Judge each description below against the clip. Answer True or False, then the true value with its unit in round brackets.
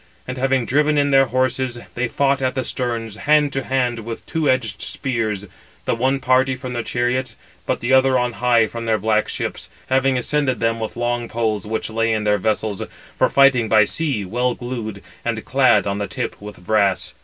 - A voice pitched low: True (120 Hz)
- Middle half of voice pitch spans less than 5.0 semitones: True (3.0 semitones)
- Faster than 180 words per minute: True (200 wpm)